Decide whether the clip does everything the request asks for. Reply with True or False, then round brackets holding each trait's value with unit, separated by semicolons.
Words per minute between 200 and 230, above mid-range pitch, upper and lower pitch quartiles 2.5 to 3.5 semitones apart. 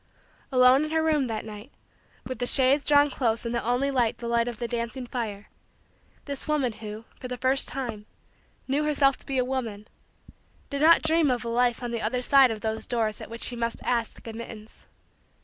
True (205 wpm; 245 Hz; 3.0 semitones)